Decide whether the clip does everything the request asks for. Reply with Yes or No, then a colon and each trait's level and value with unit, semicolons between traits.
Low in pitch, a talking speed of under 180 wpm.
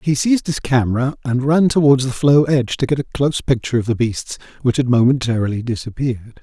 No: low, 130 Hz; fast, 205 wpm